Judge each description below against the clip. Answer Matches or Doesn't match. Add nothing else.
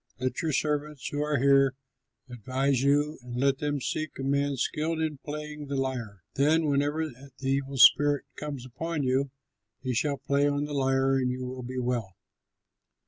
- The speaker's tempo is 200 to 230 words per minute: Doesn't match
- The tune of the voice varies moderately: Doesn't match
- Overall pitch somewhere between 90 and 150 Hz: Matches